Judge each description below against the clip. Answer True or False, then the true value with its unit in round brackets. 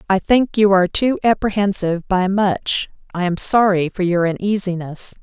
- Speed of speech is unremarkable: True (160 wpm)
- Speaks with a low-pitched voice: False (190 Hz)